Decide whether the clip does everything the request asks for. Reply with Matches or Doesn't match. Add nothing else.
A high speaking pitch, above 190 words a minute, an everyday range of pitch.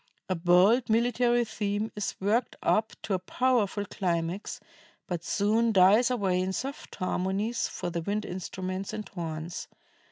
Doesn't match